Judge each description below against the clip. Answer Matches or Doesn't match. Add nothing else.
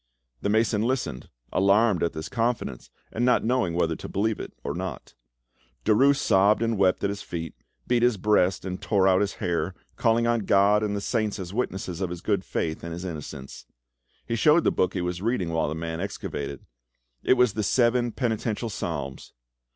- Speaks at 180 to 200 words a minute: Matches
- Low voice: Matches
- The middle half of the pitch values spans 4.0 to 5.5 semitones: Matches